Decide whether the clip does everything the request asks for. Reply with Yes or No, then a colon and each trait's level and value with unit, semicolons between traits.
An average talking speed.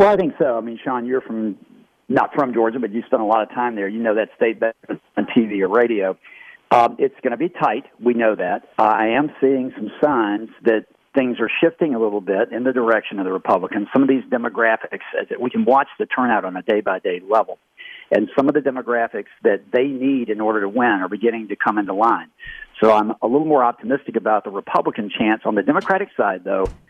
No: fast, 240 wpm